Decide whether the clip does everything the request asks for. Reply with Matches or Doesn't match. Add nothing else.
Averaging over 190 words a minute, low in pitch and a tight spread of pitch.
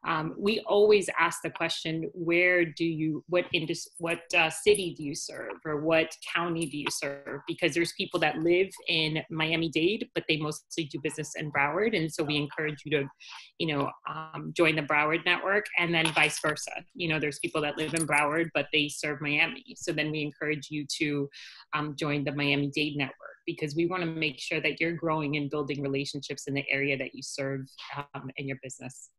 Doesn't match